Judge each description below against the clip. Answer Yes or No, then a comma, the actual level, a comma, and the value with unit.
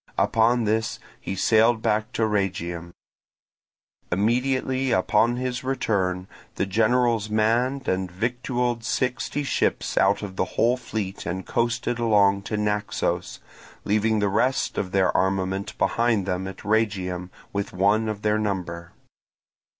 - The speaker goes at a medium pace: No, slow, 130 wpm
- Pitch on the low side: Yes, low, 105 Hz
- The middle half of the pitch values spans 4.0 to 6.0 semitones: No, average, 3.5 semitones